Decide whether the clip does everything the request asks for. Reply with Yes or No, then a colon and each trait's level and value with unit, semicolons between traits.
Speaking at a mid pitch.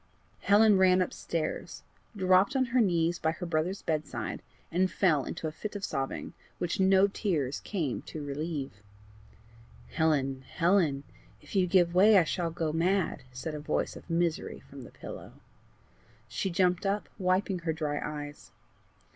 Yes: medium, 170 Hz